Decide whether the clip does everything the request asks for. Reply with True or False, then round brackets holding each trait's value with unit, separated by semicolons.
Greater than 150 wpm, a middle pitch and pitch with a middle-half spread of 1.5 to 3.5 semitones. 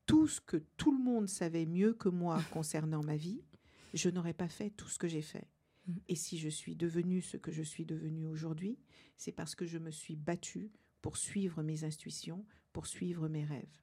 True (210 wpm; 170 Hz; 3.2 semitones)